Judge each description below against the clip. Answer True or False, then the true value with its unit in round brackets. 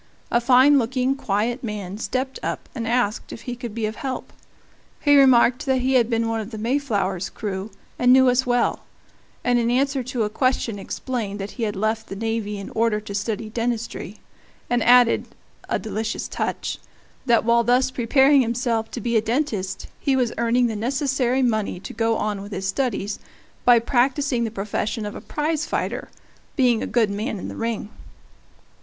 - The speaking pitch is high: True (235 Hz)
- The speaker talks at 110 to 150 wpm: False (185 wpm)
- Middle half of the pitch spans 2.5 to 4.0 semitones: True (2.9 semitones)